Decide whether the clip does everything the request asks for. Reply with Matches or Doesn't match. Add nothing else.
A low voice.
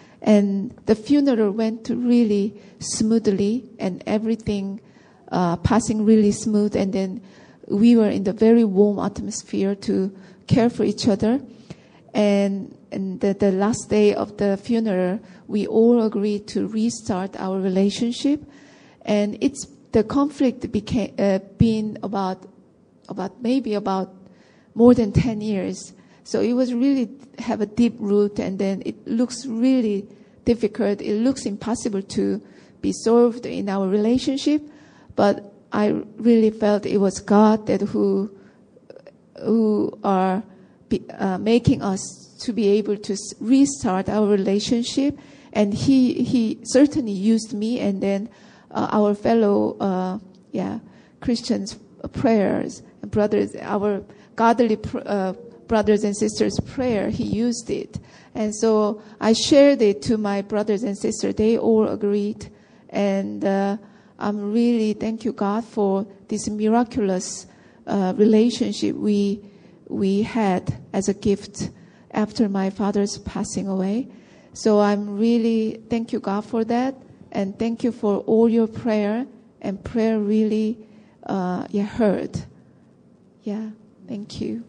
Doesn't match